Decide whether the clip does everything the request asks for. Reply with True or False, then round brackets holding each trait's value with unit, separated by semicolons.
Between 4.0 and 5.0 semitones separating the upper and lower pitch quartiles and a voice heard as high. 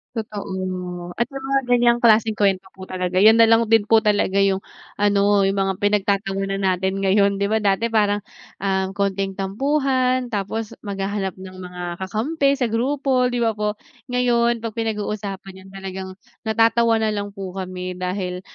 False (2.9 semitones; 205 Hz)